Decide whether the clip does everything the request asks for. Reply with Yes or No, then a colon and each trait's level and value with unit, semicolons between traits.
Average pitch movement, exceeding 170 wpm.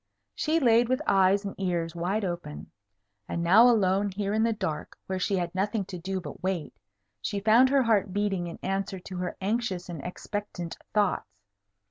Yes: average, 3.1 semitones; average, 180 wpm